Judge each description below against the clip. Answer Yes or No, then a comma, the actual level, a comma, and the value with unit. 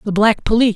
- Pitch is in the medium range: No, high, 215 Hz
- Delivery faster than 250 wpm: No, fast, 240 wpm